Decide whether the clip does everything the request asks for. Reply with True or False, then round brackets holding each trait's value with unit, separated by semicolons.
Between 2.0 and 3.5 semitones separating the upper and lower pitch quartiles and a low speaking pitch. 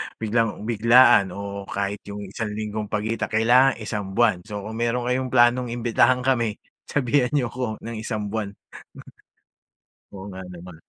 True (2.8 semitones; 110 Hz)